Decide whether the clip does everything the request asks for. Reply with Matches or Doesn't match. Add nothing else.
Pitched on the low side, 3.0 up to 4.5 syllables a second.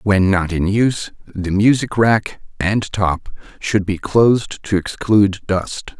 Matches